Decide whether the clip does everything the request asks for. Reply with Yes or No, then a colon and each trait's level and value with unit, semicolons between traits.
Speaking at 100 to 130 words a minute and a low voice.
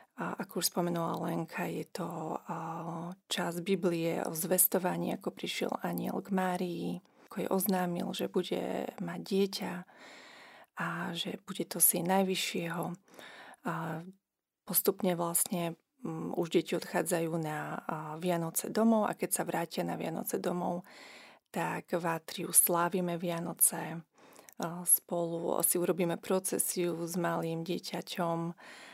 No: average, 115 wpm; medium, 175 Hz